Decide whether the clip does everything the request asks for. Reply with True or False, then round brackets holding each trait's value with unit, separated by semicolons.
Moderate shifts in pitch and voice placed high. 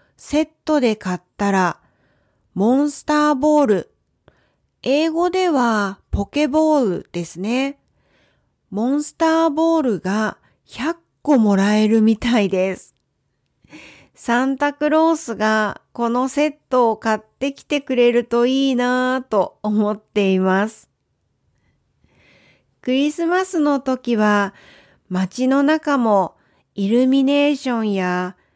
False (5.7 semitones; 245 Hz)